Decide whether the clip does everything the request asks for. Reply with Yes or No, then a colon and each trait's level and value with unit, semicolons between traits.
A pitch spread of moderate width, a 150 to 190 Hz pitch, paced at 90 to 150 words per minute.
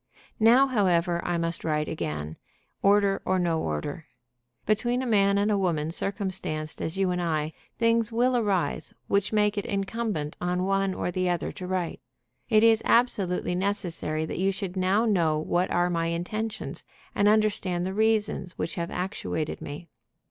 No: average, 3.7 semitones; medium, 185 Hz; average, 165 wpm